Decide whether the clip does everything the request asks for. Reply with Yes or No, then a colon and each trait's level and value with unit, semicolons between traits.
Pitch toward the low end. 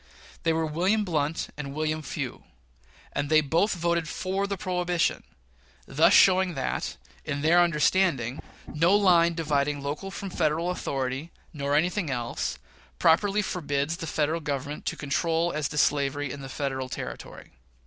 No: medium, 155 Hz